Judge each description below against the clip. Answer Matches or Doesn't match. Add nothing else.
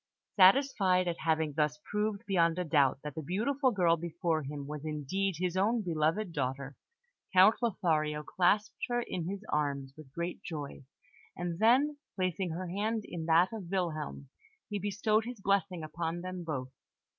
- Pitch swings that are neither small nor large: Matches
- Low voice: Doesn't match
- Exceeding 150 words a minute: Matches